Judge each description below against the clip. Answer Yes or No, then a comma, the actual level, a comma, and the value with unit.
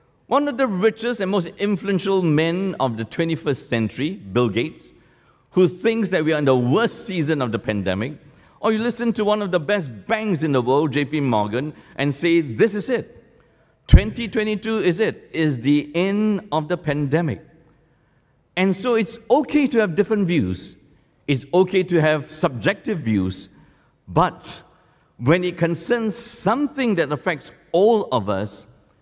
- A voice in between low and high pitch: Yes, medium, 165 Hz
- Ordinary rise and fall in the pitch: No, wide, 7.0 semitones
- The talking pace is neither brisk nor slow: Yes, average, 160 wpm